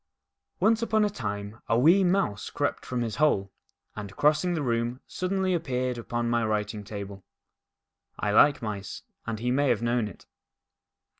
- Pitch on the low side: Yes, low, 120 Hz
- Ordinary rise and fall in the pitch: No, wide, 6.4 semitones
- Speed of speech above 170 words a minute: No, average, 160 wpm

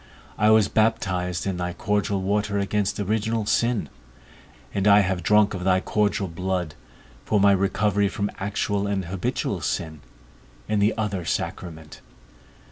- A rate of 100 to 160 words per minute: Yes, average, 140 wpm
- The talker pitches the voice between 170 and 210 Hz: No, low, 100 Hz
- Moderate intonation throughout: No, narrow, 2.1 semitones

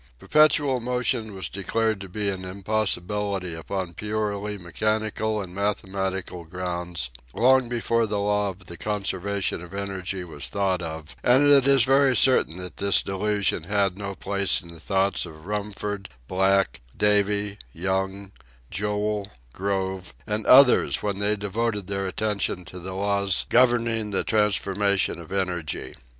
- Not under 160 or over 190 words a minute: No, average, 140 wpm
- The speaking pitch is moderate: No, low, 100 Hz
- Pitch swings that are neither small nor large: No, narrow, 2.2 semitones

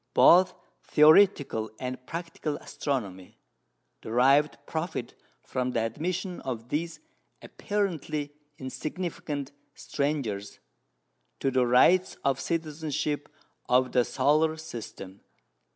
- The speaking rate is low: Yes, slow, 90 wpm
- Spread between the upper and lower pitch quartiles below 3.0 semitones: No, average, 4.3 semitones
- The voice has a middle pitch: Yes, medium, 145 Hz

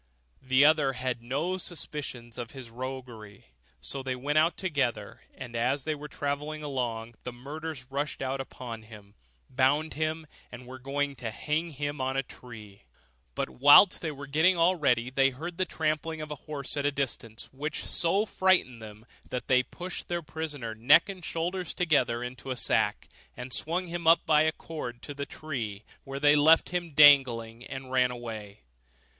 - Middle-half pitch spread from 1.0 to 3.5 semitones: No, average, 4.0 semitones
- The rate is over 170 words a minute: Yes, average, 180 wpm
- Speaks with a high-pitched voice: No, medium, 140 Hz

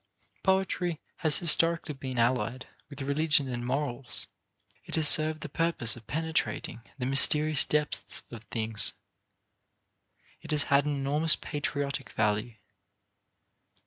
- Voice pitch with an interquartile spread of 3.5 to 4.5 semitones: Yes, average, 3.8 semitones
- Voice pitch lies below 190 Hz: Yes, medium, 140 Hz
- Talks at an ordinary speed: No, slow, 120 wpm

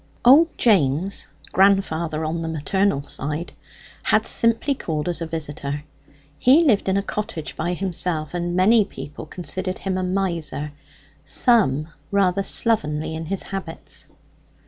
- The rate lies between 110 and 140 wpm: Yes, slow, 135 wpm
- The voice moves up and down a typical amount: Yes, average, 4.2 semitones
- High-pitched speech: No, medium, 180 Hz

